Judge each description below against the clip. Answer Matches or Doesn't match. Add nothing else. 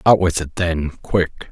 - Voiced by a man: Matches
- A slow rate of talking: Doesn't match